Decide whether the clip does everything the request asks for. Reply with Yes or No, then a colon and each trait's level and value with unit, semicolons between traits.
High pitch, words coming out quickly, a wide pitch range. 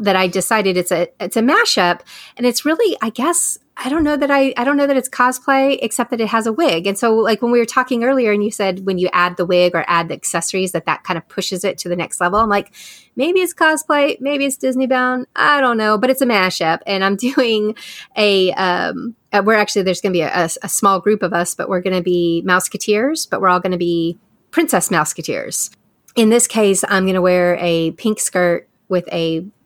Yes: high, 205 Hz; fast, 235 wpm; wide, 5.7 semitones